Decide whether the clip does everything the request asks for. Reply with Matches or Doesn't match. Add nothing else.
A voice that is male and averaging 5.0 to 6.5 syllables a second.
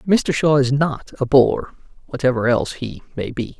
Doesn't match